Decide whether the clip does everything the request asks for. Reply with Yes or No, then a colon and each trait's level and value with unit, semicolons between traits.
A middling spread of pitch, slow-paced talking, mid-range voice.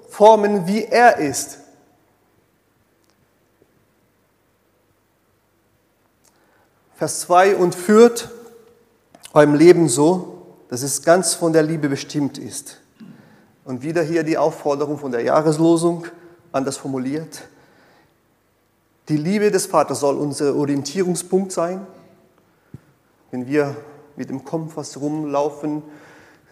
Yes: average, 3.8 semitones; slow, 95 wpm; medium, 155 Hz